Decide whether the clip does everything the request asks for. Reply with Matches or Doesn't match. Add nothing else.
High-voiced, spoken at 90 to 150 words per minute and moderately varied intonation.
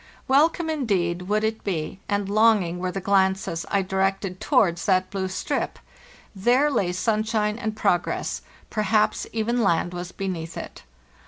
Matches